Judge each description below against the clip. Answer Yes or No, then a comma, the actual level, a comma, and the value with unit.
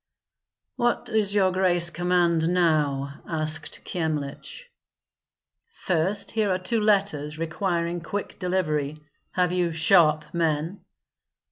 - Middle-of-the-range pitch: Yes, medium, 175 Hz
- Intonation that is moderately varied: Yes, average, 3.3 semitones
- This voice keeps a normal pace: No, slow, 105 wpm